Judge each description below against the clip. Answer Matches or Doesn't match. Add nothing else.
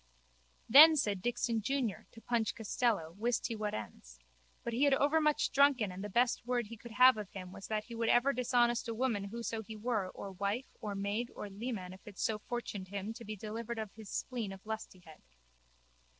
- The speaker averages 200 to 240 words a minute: Matches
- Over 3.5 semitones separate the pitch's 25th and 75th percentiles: Doesn't match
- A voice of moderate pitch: Doesn't match